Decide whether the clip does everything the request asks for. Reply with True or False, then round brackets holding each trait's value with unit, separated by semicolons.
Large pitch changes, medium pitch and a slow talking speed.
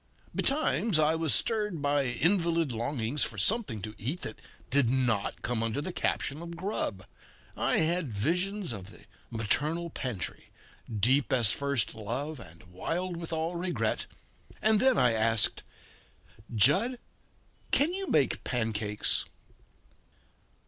True (7.3 semitones; 145 Hz; 130 wpm)